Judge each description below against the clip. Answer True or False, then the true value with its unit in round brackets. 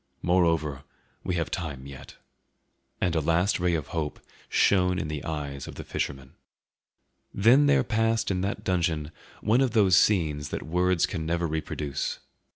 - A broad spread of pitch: False (3.9 semitones)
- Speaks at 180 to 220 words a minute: False (160 wpm)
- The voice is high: False (85 Hz)